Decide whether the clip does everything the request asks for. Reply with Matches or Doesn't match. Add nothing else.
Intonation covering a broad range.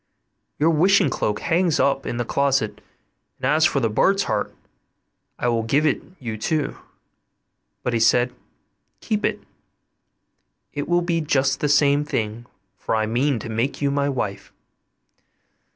Doesn't match